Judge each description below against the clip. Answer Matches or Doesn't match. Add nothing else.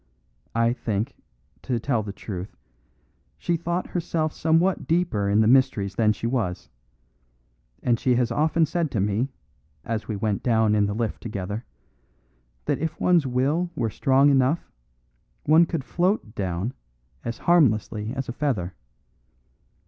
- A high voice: Doesn't match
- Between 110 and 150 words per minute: Matches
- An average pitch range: Doesn't match